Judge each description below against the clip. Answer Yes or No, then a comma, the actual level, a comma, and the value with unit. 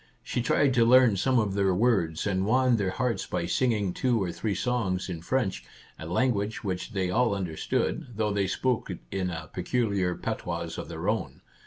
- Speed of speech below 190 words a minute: No, average, 195 wpm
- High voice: No, low, 100 Hz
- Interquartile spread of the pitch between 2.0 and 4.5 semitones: No, average, 4.9 semitones